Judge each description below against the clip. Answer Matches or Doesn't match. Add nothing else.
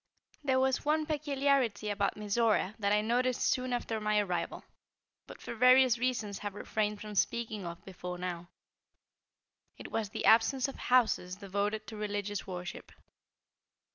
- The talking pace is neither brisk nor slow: Matches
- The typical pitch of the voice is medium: Doesn't match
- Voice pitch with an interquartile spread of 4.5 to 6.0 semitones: Doesn't match